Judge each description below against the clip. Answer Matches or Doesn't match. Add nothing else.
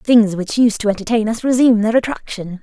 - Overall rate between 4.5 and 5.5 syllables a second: Doesn't match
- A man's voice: Doesn't match